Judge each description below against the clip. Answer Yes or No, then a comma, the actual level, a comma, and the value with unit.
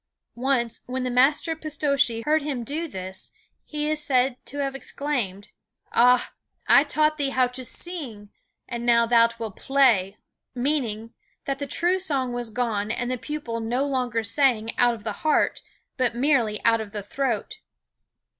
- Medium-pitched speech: No, very high, 250 Hz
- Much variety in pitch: No, average, 3.8 semitones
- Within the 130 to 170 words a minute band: Yes, average, 165 wpm